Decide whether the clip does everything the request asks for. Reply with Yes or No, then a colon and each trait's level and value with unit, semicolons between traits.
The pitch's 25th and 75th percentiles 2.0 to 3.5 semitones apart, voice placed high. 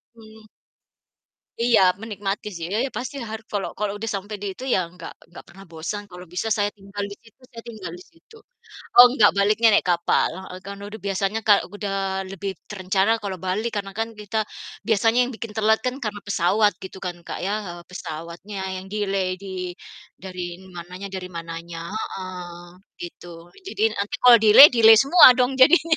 Yes: average, 2.9 semitones; high, 205 Hz